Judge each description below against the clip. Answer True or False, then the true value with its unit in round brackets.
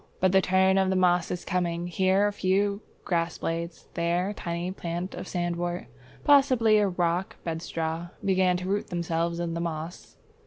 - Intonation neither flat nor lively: False (1.9 semitones)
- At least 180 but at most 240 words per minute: False (170 wpm)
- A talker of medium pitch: True (180 Hz)